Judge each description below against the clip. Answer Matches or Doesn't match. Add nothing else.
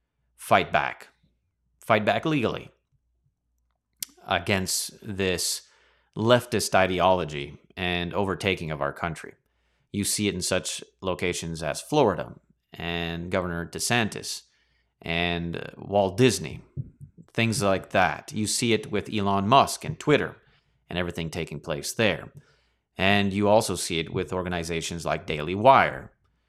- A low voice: Matches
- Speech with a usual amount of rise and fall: Matches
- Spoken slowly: Matches